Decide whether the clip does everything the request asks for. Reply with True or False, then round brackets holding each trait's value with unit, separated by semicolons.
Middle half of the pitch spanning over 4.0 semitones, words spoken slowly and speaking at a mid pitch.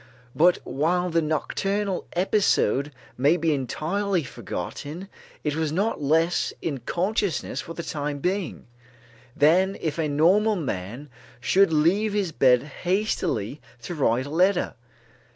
True (4.6 semitones; 130 wpm; 165 Hz)